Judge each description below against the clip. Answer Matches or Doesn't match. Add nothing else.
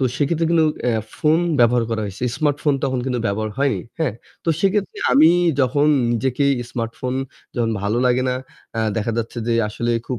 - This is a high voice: Doesn't match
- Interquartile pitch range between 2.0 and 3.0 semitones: Doesn't match